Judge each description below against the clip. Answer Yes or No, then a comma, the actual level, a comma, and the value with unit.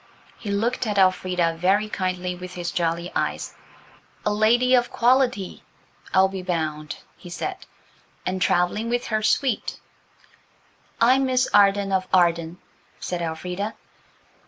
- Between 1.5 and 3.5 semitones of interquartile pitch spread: No, average, 4.0 semitones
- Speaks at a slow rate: Yes, slow, 130 wpm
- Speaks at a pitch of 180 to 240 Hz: Yes, high, 190 Hz